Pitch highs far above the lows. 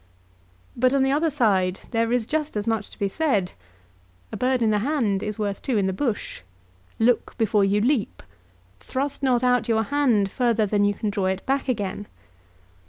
No: average, 4.3 semitones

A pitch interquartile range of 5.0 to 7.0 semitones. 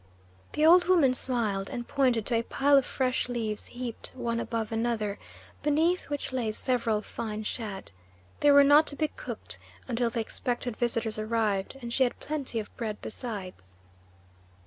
No: average, 3.8 semitones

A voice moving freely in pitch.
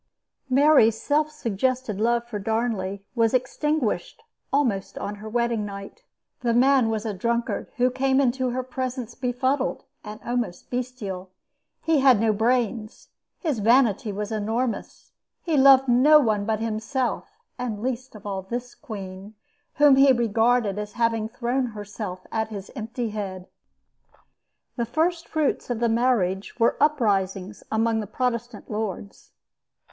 No: average, 3.4 semitones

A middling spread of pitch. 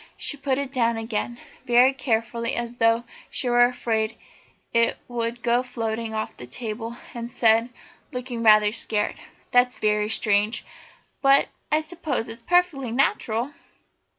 No: narrow, 2.0 semitones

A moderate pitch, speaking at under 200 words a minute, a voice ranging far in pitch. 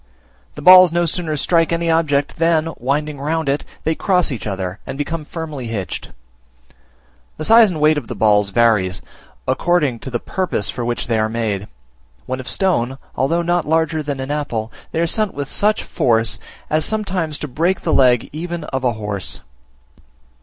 Yes: medium, 150 Hz; average, 180 wpm; wide, 5.8 semitones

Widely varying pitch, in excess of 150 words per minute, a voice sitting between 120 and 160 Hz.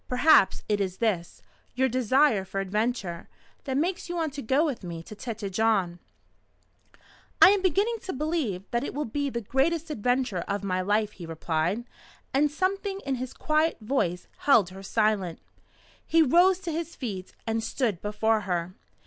No: wide, 7.4 semitones; average, 170 wpm; high, 230 Hz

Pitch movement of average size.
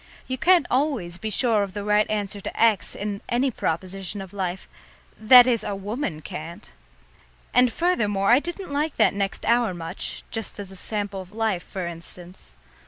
Yes: average, 4.1 semitones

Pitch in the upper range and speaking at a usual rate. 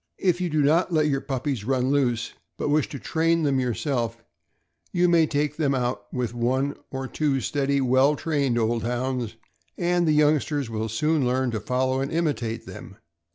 No: low, 135 Hz; average, 185 wpm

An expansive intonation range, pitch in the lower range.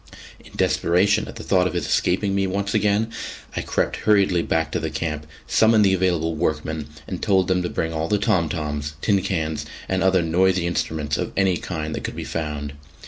No: average, 3.5 semitones; very low, 90 Hz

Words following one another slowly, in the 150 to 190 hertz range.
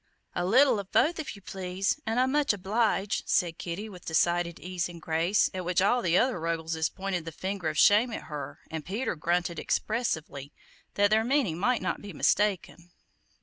No: average, 190 wpm; medium, 185 Hz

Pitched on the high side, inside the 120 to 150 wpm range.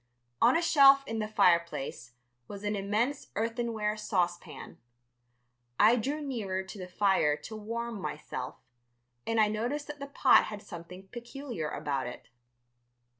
Yes: high, 215 Hz; average, 140 wpm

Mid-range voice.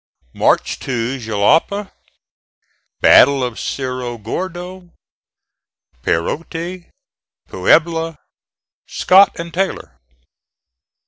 Yes: medium, 165 Hz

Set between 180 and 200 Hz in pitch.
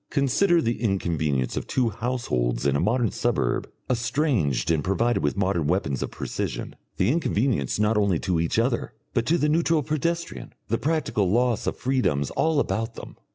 No: low, 115 Hz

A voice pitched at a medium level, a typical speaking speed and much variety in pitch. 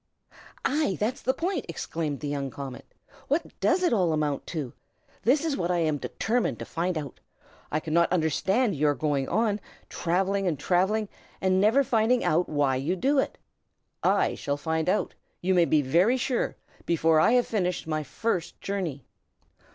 Yes: medium, 180 Hz; average, 170 wpm; wide, 6.2 semitones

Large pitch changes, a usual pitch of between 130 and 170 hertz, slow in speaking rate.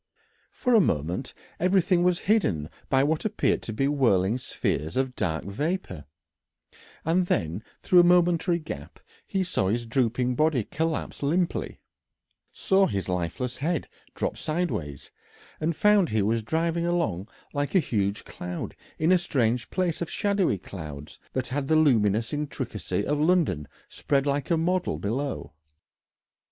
No: wide, 8.7 semitones; medium, 140 Hz; average, 145 wpm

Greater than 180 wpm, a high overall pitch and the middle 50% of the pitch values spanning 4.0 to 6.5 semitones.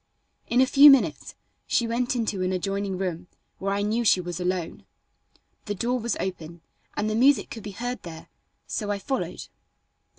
No: average, 175 wpm; high, 205 Hz; average, 4.5 semitones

